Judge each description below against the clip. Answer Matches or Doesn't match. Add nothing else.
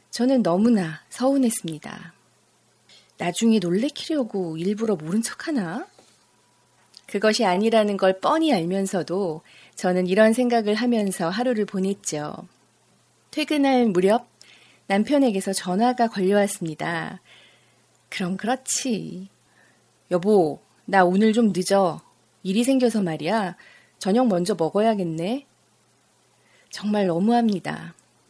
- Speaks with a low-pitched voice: Doesn't match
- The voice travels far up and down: Doesn't match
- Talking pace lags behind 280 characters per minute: Matches